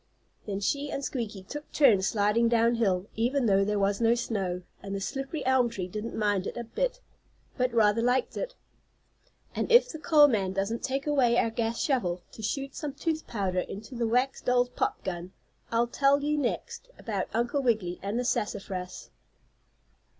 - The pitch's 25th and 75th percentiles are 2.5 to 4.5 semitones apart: No, average, 5.2 semitones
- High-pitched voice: Yes, high, 230 Hz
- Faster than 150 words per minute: Yes, average, 180 wpm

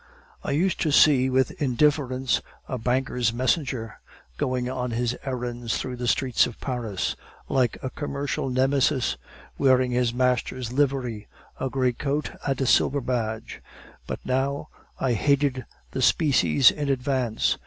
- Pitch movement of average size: No, narrow, 1.9 semitones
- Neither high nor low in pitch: No, low, 130 Hz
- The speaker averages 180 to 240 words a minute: No, average, 140 wpm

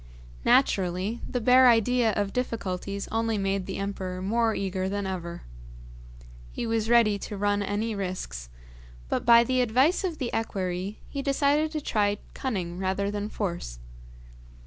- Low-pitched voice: No, high, 205 Hz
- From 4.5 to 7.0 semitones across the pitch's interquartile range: No, average, 3.7 semitones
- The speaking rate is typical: Yes, average, 145 wpm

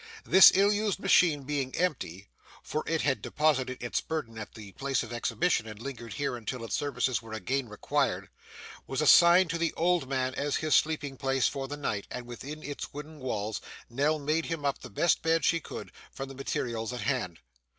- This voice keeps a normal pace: Yes, average, 195 wpm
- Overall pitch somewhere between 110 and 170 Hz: Yes, medium, 140 Hz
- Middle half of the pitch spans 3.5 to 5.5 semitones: Yes, average, 4.4 semitones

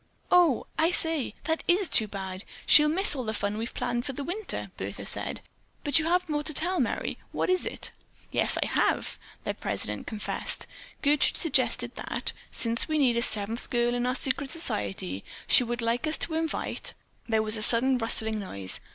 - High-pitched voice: Yes, very high, 250 Hz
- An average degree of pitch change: No, wide, 6.1 semitones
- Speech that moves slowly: No, average, 185 wpm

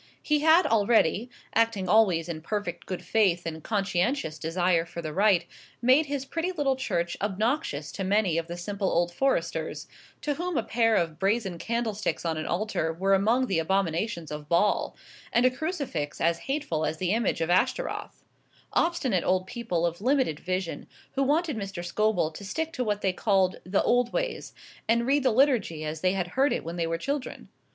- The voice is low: No, high, 200 Hz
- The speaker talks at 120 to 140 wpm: No, average, 185 wpm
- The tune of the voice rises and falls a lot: Yes, wide, 6.6 semitones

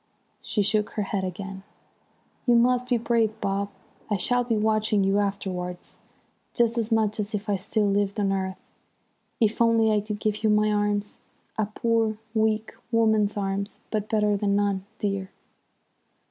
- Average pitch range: No, narrow, 1.7 semitones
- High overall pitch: Yes, high, 210 Hz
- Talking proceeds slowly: No, average, 160 wpm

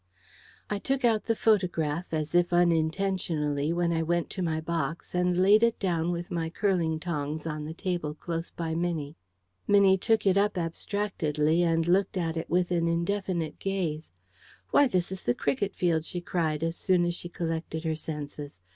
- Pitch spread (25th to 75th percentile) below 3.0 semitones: Yes, narrow, 2.5 semitones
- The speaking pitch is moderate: Yes, medium, 170 Hz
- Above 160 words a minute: Yes, average, 180 wpm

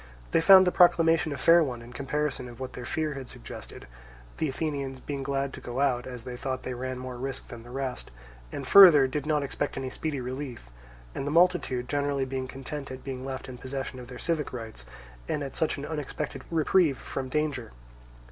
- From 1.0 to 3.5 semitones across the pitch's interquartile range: Yes, average, 2.7 semitones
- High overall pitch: No, low, 135 Hz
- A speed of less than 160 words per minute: No, fast, 205 wpm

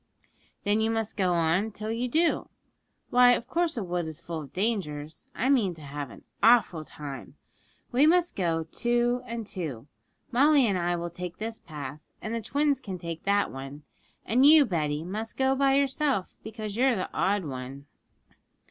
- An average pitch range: No, wide, 6.9 semitones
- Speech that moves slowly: No, average, 180 wpm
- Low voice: No, high, 205 Hz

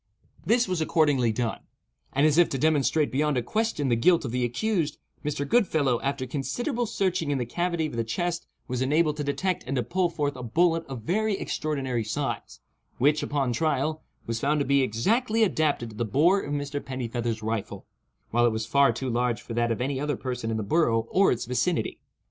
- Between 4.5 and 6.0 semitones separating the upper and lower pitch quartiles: Yes, average, 5.2 semitones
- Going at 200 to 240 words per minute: Yes, fast, 205 wpm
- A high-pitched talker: No, medium, 140 Hz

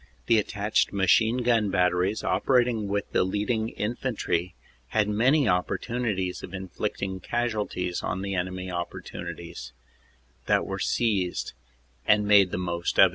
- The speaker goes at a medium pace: No, slow, 130 wpm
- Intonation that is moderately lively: Yes, average, 3.4 semitones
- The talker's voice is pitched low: Yes, low, 100 Hz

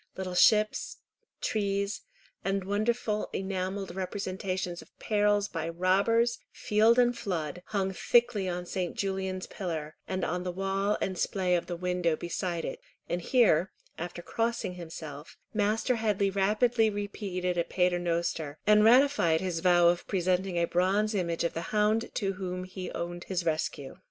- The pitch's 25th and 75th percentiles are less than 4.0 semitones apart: Yes, average, 3.0 semitones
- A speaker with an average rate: Yes, average, 150 wpm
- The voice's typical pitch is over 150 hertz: Yes, high, 190 Hz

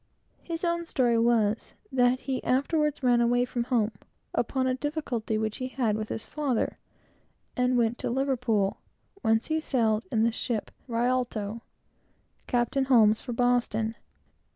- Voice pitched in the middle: No, high, 245 Hz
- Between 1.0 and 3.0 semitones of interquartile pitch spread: Yes, average, 2.7 semitones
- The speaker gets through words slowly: No, average, 145 wpm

